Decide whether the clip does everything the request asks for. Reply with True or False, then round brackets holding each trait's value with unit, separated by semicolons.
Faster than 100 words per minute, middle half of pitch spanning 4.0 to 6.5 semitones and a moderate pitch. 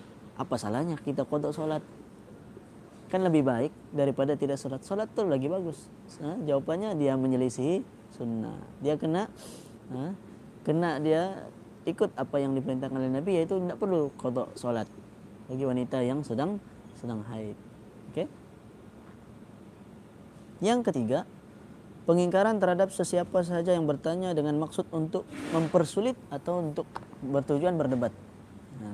True (125 wpm; 5.2 semitones; 150 Hz)